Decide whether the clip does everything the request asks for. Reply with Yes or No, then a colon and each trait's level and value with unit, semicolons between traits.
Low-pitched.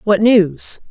No: high, 205 Hz